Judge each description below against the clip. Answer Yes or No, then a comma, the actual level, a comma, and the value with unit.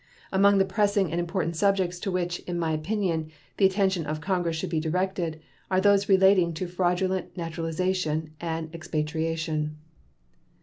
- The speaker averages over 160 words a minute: No, average, 145 wpm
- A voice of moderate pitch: Yes, medium, 175 Hz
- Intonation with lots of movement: No, average, 2.9 semitones